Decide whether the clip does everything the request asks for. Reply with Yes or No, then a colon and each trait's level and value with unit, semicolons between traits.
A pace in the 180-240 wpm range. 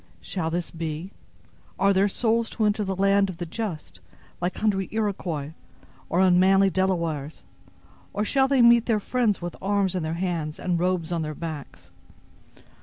No: average, 165 wpm